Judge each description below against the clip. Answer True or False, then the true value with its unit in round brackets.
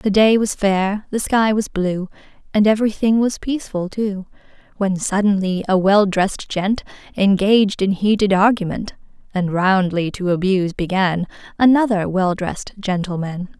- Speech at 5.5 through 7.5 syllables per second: False (4.7 syllables/s)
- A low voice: False (195 Hz)